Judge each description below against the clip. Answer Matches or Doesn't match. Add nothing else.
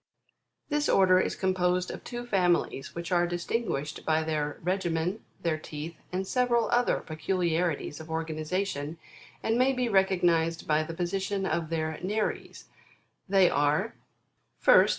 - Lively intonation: Doesn't match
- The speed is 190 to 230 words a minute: Doesn't match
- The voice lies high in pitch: Doesn't match